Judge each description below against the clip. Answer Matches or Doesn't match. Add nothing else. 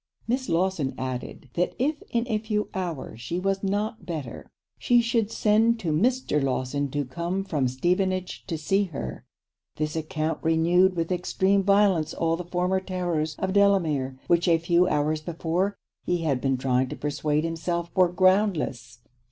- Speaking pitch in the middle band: Matches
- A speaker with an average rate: Matches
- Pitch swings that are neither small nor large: Matches